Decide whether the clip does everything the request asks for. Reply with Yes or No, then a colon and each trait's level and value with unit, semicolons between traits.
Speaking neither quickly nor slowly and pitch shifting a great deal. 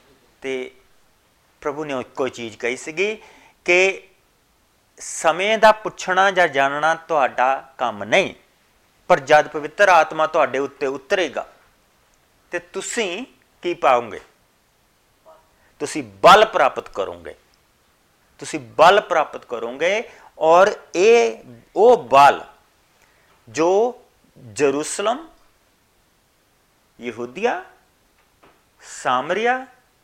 No: slow, 85 wpm; wide, 7.0 semitones